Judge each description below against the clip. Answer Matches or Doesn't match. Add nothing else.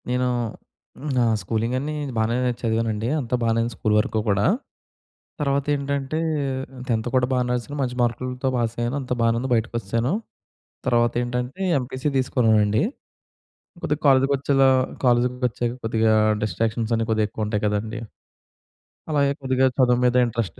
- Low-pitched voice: Matches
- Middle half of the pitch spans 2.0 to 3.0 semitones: Matches